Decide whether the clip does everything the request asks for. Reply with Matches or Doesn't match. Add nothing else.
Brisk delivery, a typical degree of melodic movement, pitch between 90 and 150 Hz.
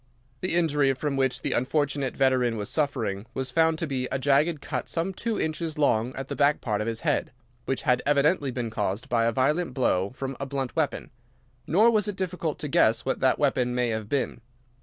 Matches